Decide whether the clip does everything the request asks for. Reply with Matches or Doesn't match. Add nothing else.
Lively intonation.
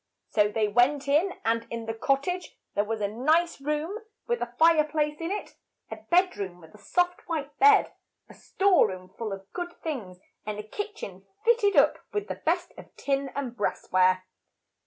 Matches